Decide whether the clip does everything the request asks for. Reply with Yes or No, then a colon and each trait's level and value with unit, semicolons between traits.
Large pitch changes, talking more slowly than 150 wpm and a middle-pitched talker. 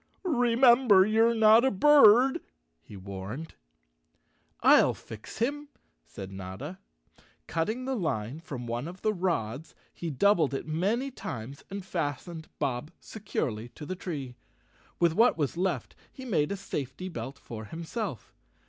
Yes: wide, 9.0 semitones; average, 140 wpm; medium, 170 Hz